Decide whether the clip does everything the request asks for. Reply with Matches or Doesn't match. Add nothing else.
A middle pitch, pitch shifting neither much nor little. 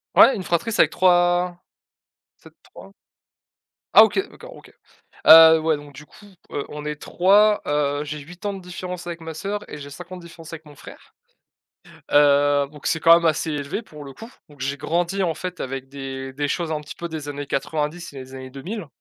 Matches